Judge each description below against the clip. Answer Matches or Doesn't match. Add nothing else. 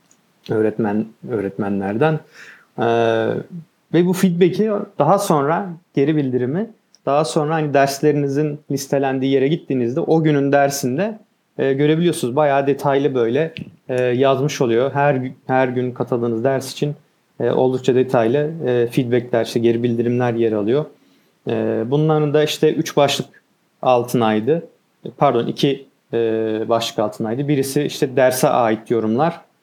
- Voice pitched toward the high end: Doesn't match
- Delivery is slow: Doesn't match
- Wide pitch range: Doesn't match